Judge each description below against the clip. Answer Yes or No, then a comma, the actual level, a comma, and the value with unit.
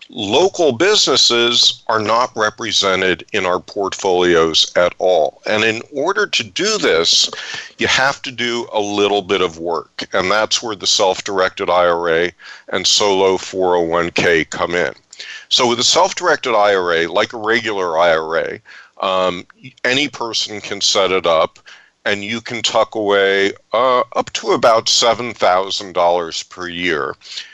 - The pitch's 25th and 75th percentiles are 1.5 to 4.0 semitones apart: No, average, 4.7 semitones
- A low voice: Yes, low, 100 Hz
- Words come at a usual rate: Yes, average, 145 wpm